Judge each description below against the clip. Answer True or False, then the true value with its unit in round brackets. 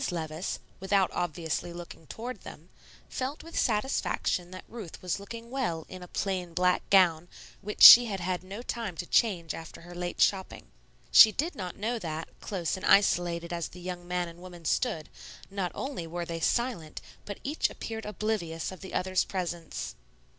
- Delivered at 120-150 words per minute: False (175 wpm)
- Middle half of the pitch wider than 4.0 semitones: False (3.5 semitones)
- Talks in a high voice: False (180 Hz)